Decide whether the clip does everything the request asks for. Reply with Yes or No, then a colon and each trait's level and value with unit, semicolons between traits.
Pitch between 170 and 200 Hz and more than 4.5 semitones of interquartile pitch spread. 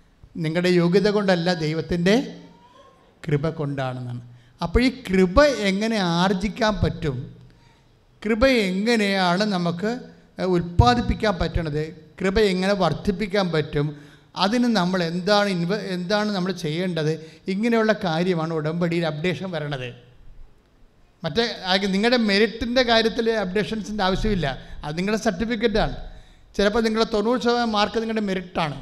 Yes: medium, 185 Hz; wide, 5.4 semitones